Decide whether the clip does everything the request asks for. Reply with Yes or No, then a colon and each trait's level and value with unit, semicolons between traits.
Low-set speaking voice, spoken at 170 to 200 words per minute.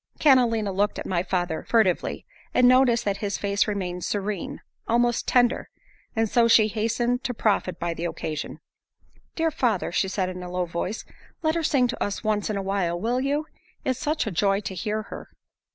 No: high, 210 Hz; average, 190 wpm